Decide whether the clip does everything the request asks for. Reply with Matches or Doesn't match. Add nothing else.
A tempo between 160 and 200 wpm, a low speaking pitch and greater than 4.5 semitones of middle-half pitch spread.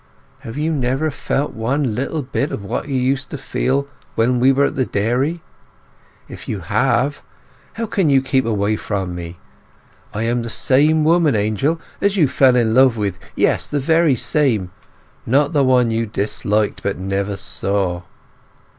Matches